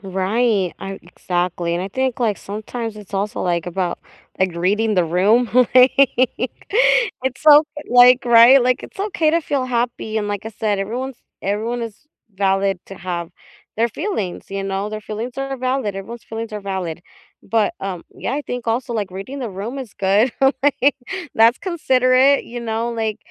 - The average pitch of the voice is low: No, high, 225 Hz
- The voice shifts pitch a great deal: No, average, 4.6 semitones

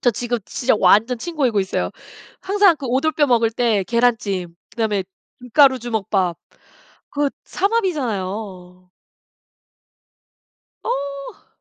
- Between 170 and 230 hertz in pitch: No, high, 240 Hz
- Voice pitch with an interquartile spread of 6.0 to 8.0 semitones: No, wide, 5.6 semitones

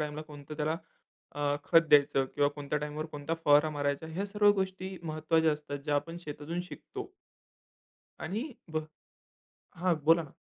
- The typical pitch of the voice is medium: Yes, medium, 155 Hz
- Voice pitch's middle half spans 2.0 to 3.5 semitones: Yes, narrow, 2.4 semitones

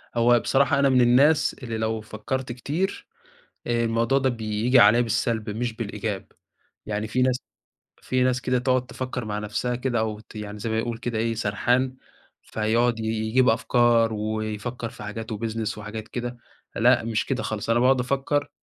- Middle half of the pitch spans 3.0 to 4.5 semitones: No, narrow, 2.5 semitones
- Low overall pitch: Yes, low, 115 Hz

